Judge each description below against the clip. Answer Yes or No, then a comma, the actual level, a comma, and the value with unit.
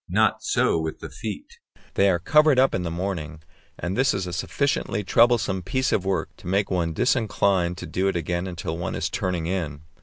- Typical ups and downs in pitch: Yes, average, 3.0 semitones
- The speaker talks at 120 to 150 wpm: No, fast, 205 wpm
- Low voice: Yes, very low, 95 Hz